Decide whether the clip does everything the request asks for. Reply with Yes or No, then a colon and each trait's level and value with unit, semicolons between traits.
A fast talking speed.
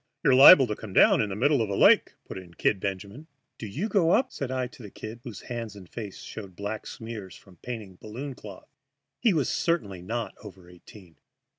Yes: fast, 210 wpm